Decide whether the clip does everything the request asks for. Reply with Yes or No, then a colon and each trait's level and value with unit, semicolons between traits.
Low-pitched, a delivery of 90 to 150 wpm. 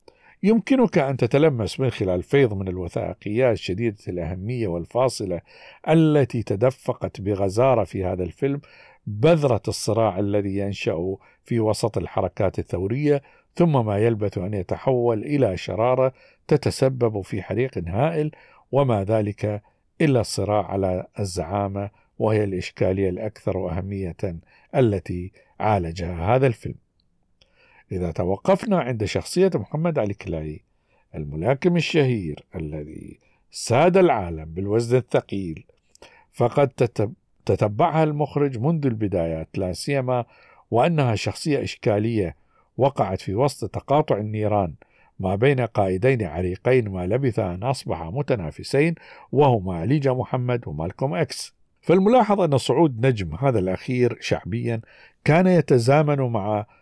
Yes: low, 110 Hz; average, 110 wpm